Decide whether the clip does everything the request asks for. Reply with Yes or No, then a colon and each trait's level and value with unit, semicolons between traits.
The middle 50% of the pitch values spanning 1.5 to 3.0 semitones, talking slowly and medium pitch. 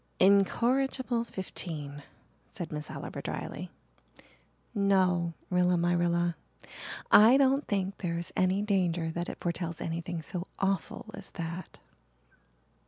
Yes: average, 2.7 semitones; slow, 115 wpm; medium, 180 Hz